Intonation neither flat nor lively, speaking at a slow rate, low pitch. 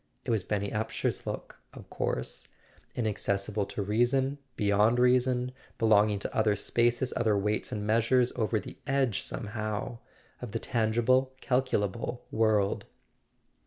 Yes: average, 3.0 semitones; slow, 125 wpm; low, 110 Hz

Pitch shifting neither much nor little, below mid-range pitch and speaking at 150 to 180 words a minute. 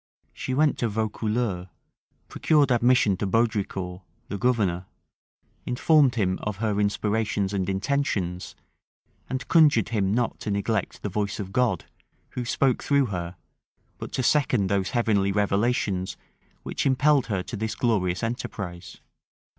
No: average, 4.2 semitones; low, 105 Hz; slow, 135 wpm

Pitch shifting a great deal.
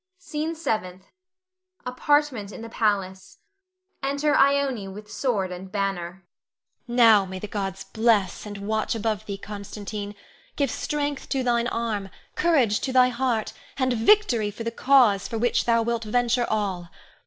No: average, 3.9 semitones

